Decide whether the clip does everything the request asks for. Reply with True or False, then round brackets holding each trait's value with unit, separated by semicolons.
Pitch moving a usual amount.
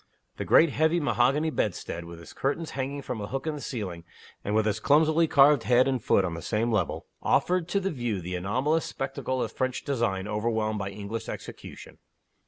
False (5.9 semitones)